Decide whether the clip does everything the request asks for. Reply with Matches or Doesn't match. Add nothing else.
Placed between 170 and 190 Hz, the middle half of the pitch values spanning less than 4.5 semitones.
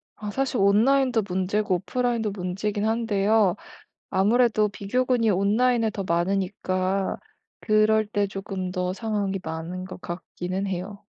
Doesn't match